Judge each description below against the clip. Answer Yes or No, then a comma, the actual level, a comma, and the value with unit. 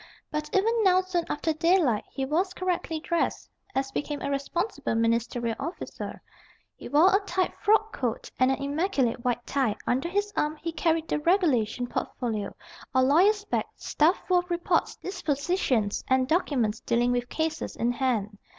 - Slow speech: No, average, 160 wpm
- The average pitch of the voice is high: Yes, very high, 300 Hz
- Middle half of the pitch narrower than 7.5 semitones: Yes, wide, 6.4 semitones